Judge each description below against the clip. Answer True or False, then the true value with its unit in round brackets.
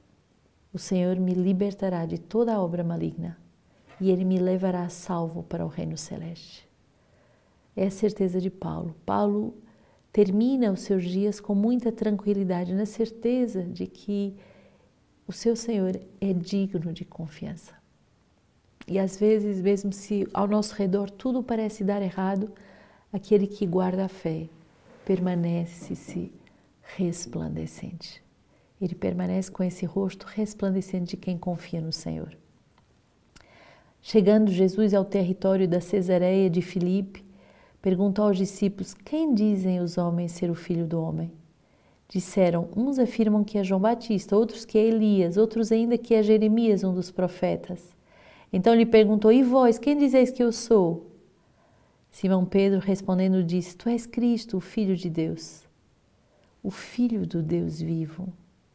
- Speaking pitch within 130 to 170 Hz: False (190 Hz)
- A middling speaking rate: True (140 wpm)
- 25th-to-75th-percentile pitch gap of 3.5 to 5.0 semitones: False (2.9 semitones)